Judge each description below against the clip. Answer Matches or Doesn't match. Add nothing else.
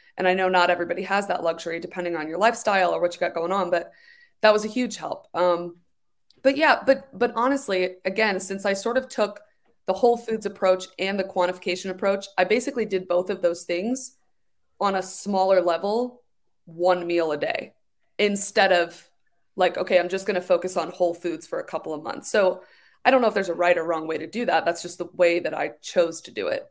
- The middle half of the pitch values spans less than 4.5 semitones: Matches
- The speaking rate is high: Matches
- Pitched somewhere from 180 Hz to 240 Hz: Matches